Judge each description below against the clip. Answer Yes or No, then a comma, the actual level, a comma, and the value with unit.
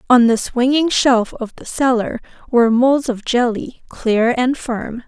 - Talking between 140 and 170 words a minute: Yes, average, 165 wpm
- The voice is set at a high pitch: Yes, high, 245 Hz